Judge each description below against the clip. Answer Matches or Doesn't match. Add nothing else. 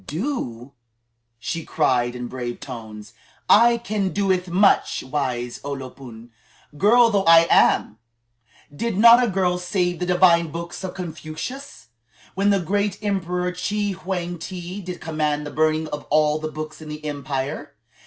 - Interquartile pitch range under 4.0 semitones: Doesn't match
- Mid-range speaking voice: Matches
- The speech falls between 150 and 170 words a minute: Matches